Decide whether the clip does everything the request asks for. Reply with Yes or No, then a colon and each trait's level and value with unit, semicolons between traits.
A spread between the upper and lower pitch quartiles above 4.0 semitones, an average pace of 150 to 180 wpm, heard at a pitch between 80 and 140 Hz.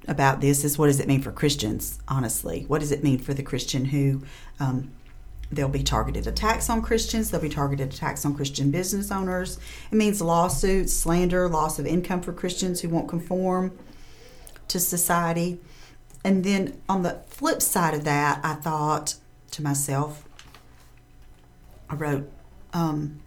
No: average, 4.4 semitones; average, 160 wpm; medium, 150 Hz